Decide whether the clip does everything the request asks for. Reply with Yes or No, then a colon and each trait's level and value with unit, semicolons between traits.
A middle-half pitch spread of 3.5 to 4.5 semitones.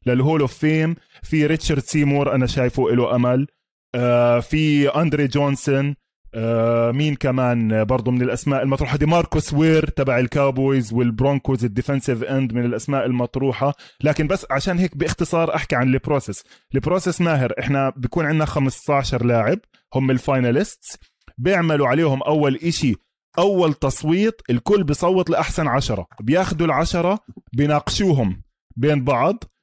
Yes: average, 3.8 semitones